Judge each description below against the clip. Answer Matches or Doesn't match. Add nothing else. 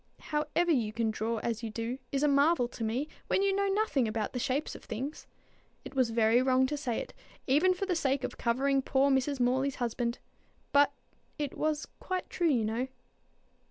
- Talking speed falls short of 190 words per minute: Doesn't match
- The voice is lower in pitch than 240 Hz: Doesn't match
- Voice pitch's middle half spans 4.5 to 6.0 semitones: Doesn't match